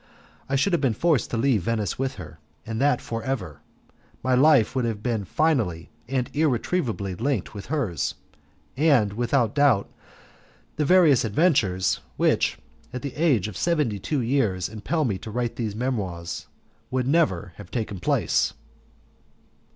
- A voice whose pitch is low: Yes, low, 120 Hz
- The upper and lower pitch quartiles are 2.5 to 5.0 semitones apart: No, wide, 5.5 semitones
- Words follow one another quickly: No, average, 150 wpm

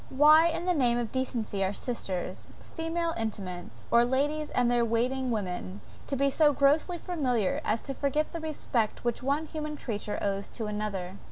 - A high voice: Yes, very high, 250 Hz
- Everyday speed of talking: Yes, average, 175 wpm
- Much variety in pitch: Yes, wide, 6.0 semitones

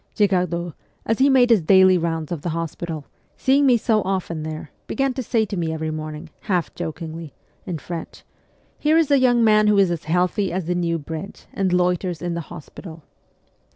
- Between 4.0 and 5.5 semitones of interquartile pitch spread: Yes, average, 4.5 semitones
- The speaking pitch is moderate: Yes, medium, 180 Hz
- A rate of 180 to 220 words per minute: Yes, average, 195 wpm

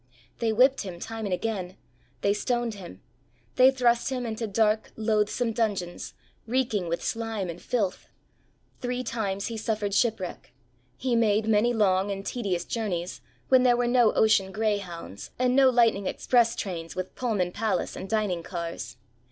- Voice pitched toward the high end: Yes, high, 215 Hz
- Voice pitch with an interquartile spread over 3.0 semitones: Yes, average, 3.7 semitones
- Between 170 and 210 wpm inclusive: No, average, 155 wpm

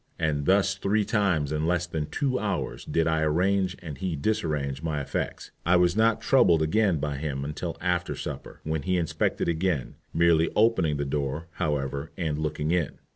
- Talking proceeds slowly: No, average, 180 wpm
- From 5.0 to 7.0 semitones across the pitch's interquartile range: No, average, 3.7 semitones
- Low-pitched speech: Yes, very low, 80 Hz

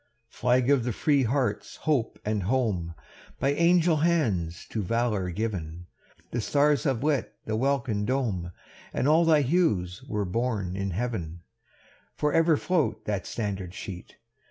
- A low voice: Yes, low, 115 Hz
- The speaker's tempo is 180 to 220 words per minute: No, average, 150 wpm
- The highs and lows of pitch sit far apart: Yes, wide, 6.5 semitones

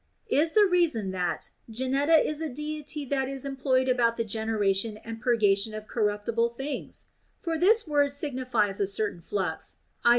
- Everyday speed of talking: Yes, average, 160 wpm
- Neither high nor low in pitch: No, high, 245 Hz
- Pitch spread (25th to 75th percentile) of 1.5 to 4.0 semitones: No, average, 5.2 semitones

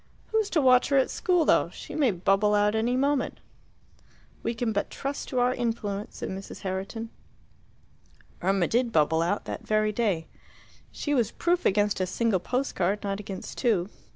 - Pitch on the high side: Yes, high, 215 Hz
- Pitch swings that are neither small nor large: Yes, average, 4.4 semitones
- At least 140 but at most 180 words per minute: Yes, average, 175 wpm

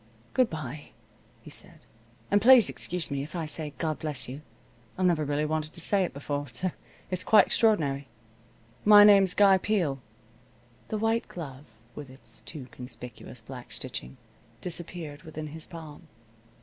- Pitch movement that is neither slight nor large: Yes, average, 4.8 semitones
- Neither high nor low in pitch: Yes, medium, 155 Hz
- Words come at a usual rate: Yes, average, 155 wpm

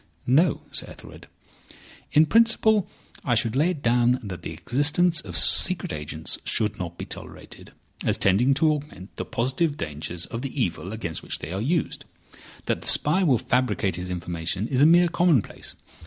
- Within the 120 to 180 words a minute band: Yes, average, 170 wpm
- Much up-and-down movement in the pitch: Yes, wide, 8.7 semitones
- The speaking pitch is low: Yes, low, 125 Hz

